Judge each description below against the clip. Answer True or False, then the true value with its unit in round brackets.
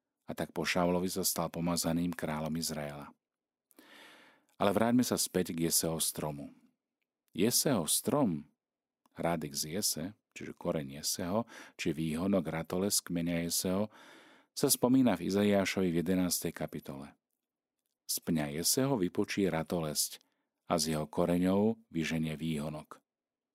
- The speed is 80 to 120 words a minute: True (115 wpm)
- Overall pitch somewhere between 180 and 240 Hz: False (85 Hz)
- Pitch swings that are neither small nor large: True (3.1 semitones)